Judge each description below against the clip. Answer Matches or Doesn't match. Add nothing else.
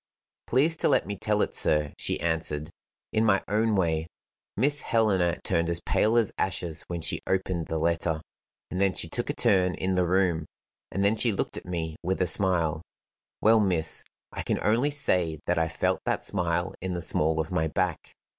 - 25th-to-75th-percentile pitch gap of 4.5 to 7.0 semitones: Doesn't match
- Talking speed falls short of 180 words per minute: Doesn't match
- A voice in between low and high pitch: Doesn't match